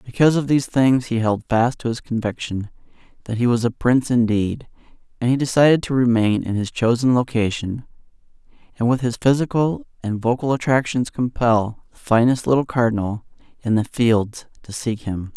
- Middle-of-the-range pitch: No, low, 120 Hz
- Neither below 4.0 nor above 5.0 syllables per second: No, 5.2 syllables/s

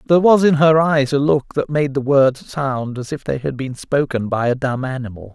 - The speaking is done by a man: Yes, male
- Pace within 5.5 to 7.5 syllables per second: No, 5.1 syllables/s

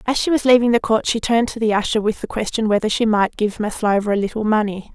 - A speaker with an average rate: No, fast, 265 wpm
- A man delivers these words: No, female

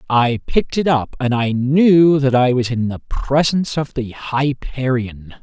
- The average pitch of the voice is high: No, low, 130 Hz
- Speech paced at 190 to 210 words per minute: No, average, 175 wpm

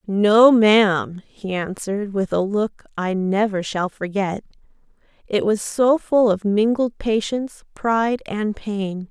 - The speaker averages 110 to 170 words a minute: Yes, average, 140 wpm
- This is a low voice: No, high, 210 Hz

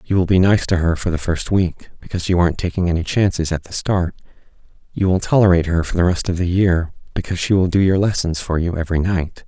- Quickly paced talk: Yes, fast, 245 wpm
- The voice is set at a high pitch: No, very low, 90 Hz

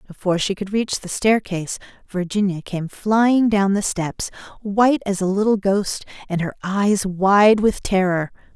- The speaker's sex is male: No, female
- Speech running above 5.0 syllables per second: No, 4.4 syllables/s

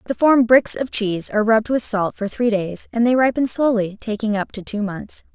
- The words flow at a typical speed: No, fast, 235 wpm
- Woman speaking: Yes, female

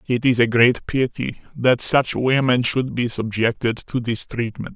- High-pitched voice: No, low, 120 Hz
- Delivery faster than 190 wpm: No, average, 175 wpm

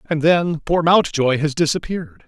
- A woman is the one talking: No, male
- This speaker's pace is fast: No, average, 160 wpm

